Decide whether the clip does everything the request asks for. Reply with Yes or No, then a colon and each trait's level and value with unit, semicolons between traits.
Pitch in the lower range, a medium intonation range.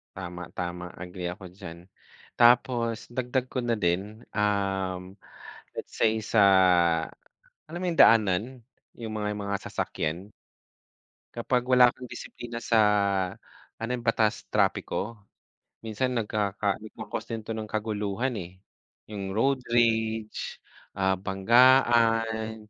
Yes: low, 110 Hz; average, 3.4 semitones